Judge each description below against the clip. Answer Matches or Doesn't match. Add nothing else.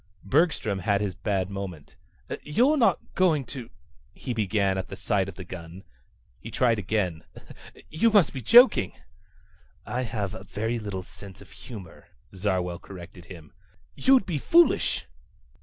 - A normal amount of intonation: Doesn't match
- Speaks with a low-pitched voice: Matches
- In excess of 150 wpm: Doesn't match